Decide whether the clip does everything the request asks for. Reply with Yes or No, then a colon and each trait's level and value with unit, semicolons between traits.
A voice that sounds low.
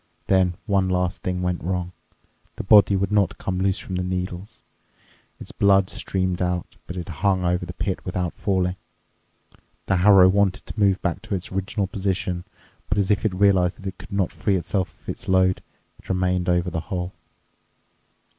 Yes: very low, 95 Hz